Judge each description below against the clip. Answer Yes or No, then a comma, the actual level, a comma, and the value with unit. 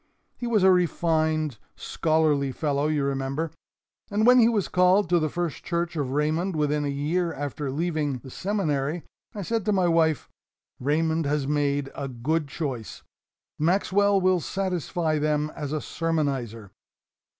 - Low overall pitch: No, medium, 155 Hz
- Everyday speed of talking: Yes, average, 150 wpm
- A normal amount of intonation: Yes, average, 3.6 semitones